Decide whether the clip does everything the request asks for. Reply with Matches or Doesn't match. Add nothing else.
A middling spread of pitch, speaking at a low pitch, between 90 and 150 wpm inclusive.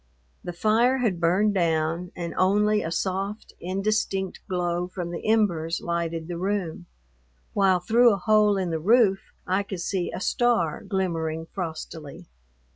Doesn't match